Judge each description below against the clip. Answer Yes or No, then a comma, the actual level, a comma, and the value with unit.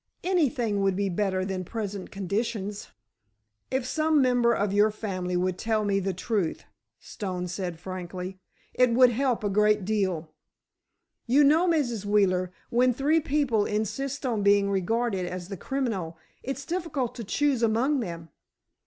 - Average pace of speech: Yes, average, 150 wpm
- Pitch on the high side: Yes, high, 210 Hz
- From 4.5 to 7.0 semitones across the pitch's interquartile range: Yes, average, 5.1 semitones